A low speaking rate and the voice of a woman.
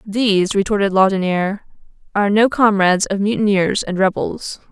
Yes: slow, 125 wpm; female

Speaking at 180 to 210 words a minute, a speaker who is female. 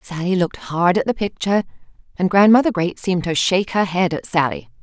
Yes: average, 200 wpm; female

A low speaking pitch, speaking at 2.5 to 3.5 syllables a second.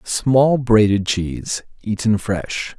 Yes: low, 110 Hz; 3.2 syllables/s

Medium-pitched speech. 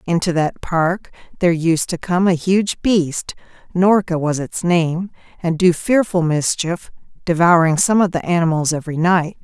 Yes: medium, 170 Hz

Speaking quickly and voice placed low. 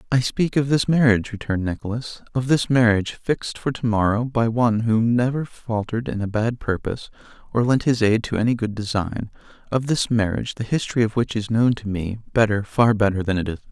Yes: fast, 215 wpm; low, 115 Hz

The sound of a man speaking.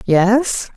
No: female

